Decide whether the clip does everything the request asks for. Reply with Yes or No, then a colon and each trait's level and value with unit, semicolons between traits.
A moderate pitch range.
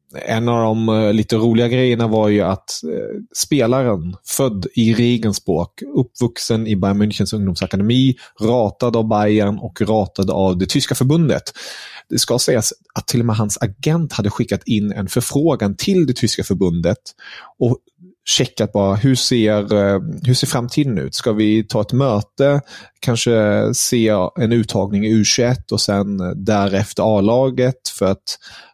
Yes: average, 3.5 semitones